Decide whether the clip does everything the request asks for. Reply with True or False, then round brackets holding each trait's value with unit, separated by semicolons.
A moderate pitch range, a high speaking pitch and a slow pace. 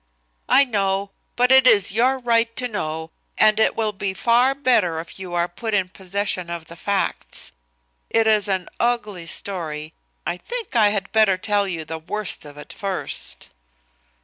False (4.5 semitones; 200 Hz; 175 wpm)